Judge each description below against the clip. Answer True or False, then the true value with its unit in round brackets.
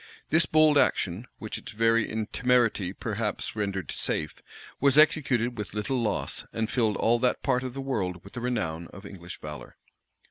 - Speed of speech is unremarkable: True (170 wpm)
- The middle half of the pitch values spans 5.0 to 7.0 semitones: False (4.2 semitones)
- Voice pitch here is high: False (115 Hz)